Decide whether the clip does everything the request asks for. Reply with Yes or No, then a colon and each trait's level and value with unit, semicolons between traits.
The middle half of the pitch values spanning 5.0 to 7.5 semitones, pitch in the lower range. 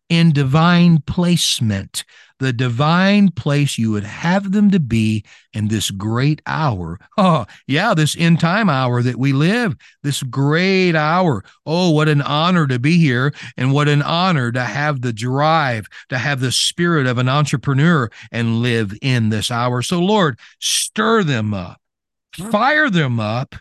No: wide, 5.4 semitones; medium, 145 Hz